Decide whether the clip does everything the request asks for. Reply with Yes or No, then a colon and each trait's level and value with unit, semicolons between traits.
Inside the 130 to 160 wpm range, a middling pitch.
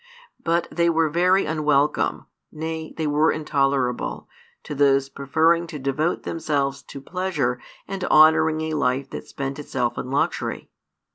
Yes: average, 140 wpm; medium, 150 Hz